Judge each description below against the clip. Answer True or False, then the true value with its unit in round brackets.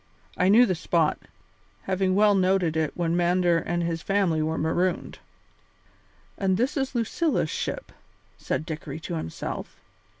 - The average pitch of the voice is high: False (180 Hz)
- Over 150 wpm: False (140 wpm)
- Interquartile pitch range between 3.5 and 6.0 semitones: False (3.1 semitones)